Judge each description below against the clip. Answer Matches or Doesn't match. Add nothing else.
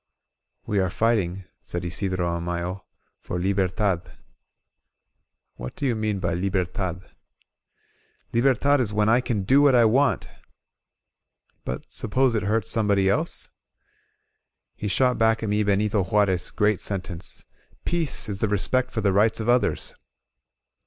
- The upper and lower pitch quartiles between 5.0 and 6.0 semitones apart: Doesn't match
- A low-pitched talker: Matches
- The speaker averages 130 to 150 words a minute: Matches